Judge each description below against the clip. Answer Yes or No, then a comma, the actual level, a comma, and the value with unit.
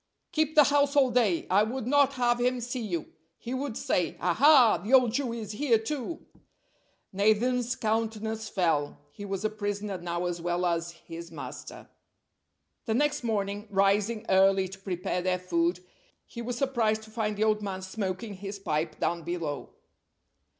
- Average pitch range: Yes, average, 4.7 semitones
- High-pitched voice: Yes, high, 215 Hz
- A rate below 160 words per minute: No, average, 165 wpm